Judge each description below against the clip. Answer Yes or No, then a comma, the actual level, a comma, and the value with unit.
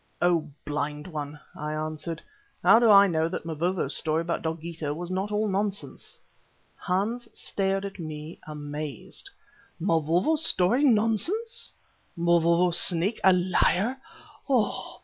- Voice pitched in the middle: Yes, medium, 175 Hz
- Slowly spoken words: Yes, slow, 120 wpm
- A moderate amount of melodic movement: Yes, average, 4.3 semitones